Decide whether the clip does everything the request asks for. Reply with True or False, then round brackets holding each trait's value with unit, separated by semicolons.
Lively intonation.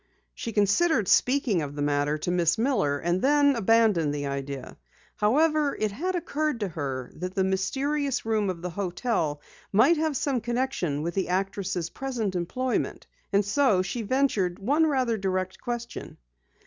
True (7.0 semitones)